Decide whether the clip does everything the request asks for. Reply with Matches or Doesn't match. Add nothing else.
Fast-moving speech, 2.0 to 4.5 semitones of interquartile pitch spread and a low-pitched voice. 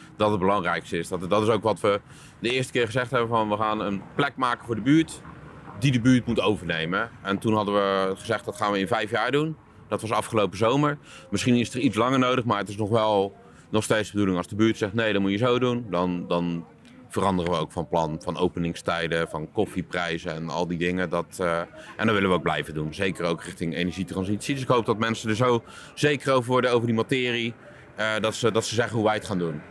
Doesn't match